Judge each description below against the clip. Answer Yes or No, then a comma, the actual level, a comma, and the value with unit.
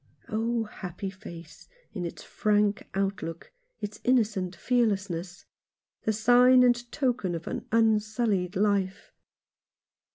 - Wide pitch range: No, average, 3.5 semitones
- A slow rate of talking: Yes, slow, 110 wpm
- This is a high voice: Yes, high, 210 Hz